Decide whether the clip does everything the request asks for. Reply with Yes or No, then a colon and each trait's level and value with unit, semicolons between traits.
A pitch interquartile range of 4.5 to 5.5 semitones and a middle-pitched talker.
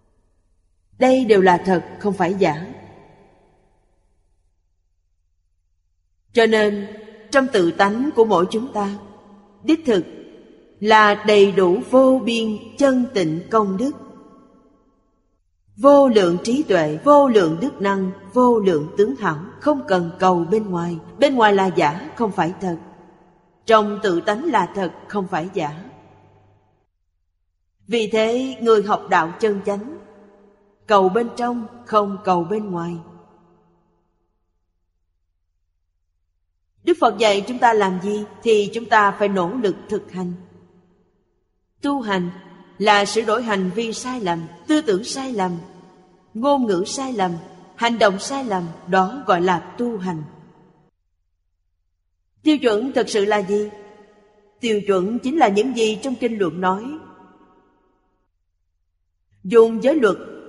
No: average, 5.1 semitones; high, 195 Hz